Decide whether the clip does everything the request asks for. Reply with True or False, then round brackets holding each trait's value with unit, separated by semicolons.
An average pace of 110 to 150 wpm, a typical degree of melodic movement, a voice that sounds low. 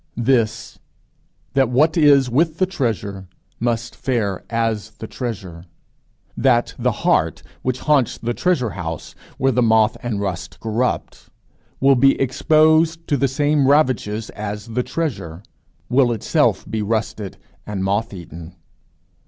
True (135 wpm; 4.7 semitones; 120 Hz)